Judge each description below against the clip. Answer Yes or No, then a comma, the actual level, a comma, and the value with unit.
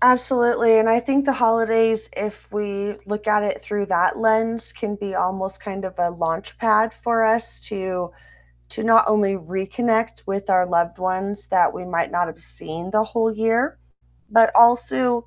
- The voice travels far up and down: No, average, 3.2 semitones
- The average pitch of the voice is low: No, high, 210 Hz